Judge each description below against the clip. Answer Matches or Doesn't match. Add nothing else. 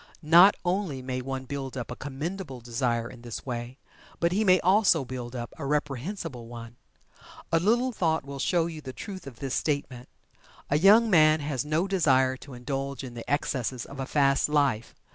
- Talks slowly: Doesn't match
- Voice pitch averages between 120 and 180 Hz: Matches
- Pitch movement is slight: Doesn't match